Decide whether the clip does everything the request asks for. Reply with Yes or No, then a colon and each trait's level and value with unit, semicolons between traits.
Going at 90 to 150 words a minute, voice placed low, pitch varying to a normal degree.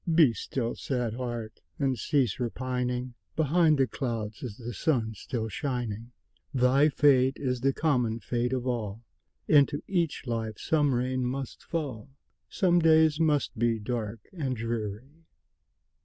Yes: average, 140 wpm; low, 125 Hz; average, 3.8 semitones